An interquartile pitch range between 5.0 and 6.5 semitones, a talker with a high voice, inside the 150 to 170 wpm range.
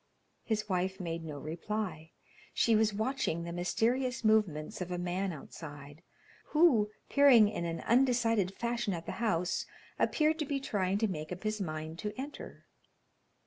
Yes: wide, 5.5 semitones; high, 200 Hz; average, 155 wpm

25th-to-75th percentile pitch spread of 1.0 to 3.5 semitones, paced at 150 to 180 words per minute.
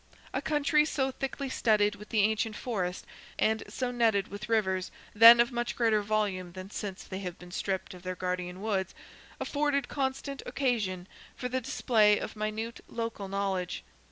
No: average, 4.0 semitones; average, 165 wpm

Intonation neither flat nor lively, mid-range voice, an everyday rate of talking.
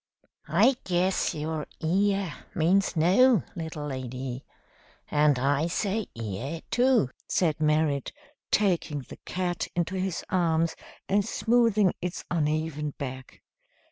No: average, 4.5 semitones; medium, 165 Hz; slow, 110 wpm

